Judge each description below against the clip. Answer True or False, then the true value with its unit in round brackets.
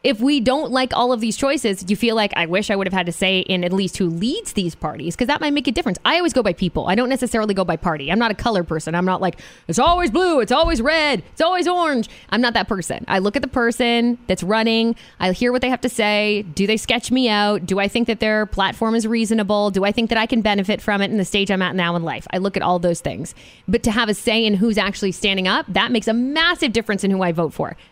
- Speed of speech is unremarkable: False (290 wpm)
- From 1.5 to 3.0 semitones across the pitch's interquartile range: False (4.4 semitones)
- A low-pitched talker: False (215 Hz)